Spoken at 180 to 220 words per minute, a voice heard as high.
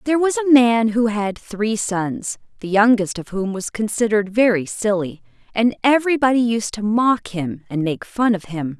Yes: average, 185 wpm; high, 220 Hz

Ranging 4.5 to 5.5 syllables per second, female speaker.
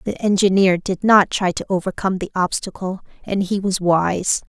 Yes: 5.0 syllables/s; female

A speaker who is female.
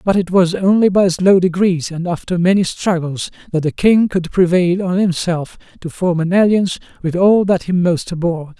No: male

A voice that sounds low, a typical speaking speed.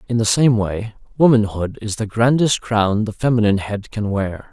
Yes: low, 110 Hz; average, 185 wpm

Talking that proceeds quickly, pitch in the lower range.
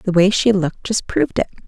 No: fast, 250 wpm; high, 190 Hz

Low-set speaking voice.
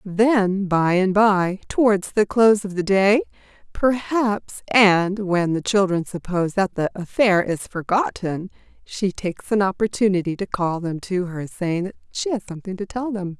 No: high, 195 Hz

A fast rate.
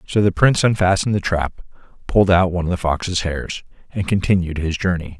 No: average, 195 wpm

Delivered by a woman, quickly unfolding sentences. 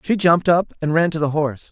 No: male; fast, 280 wpm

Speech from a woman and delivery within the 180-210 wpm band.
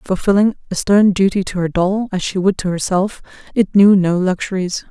Yes: female; average, 195 wpm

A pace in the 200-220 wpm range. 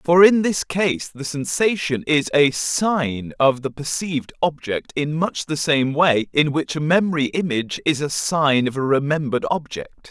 No: average, 180 wpm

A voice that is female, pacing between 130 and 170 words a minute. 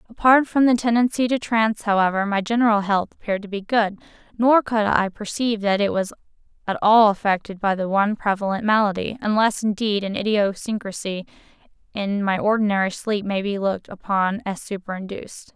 Yes: female; average, 160 wpm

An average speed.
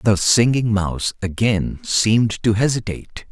No: slow, 125 wpm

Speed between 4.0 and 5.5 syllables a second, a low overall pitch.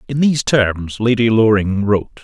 Yes: 5.2 syllables/s; low, 115 Hz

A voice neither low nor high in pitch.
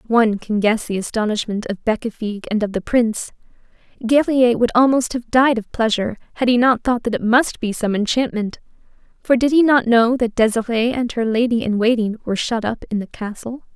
No: high, 230 Hz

